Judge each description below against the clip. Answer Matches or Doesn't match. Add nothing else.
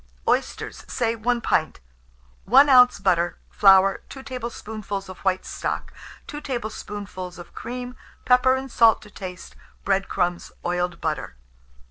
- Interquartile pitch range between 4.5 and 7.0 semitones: Matches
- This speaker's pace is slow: Matches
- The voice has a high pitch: Matches